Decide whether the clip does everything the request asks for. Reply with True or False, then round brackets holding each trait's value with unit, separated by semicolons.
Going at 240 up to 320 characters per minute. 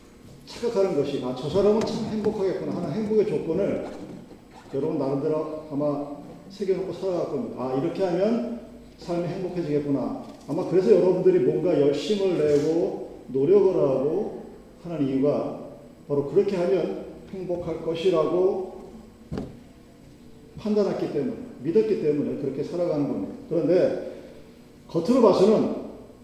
True (300 characters per minute)